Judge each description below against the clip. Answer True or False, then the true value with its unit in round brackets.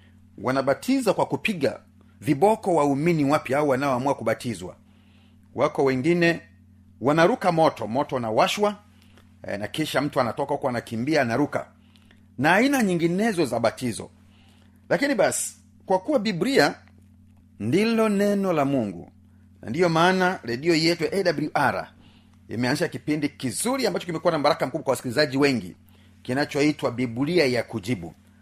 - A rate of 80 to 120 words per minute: False (130 wpm)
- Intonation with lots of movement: True (8.8 semitones)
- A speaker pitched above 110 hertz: True (135 Hz)